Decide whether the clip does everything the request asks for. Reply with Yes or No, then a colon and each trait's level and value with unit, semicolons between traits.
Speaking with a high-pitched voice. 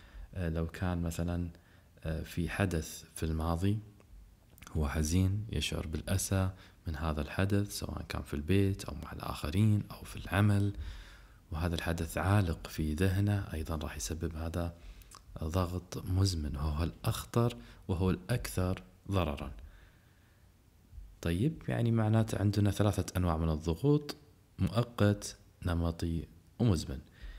No: very low, 90 Hz